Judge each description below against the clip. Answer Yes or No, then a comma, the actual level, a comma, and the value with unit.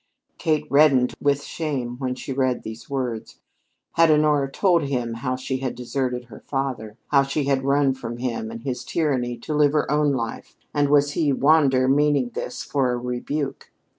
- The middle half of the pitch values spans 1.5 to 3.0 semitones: Yes, average, 2.7 semitones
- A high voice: No, low, 135 Hz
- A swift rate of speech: No, average, 180 wpm